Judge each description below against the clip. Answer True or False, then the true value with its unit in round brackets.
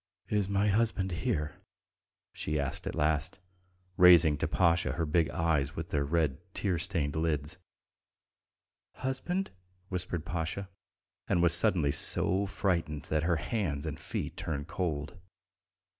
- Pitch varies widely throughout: False (3.5 semitones)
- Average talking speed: False (130 wpm)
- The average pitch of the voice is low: True (85 Hz)